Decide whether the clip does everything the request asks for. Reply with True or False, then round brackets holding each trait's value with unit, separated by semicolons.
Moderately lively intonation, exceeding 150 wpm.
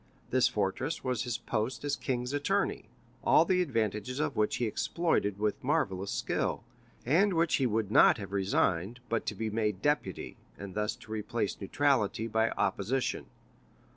True (4.2 semitones; 160 wpm)